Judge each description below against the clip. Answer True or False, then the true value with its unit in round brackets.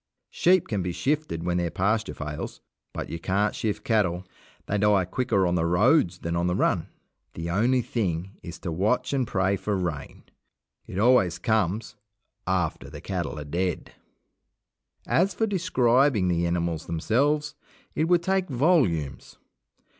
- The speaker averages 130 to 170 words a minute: True (155 wpm)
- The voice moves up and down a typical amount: False (6.7 semitones)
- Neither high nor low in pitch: False (95 Hz)